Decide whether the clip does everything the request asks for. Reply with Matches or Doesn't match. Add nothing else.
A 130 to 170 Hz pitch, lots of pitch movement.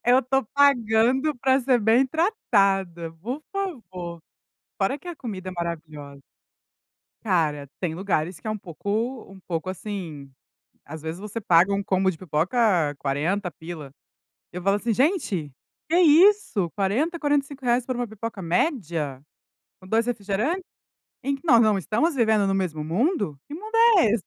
Doesn't match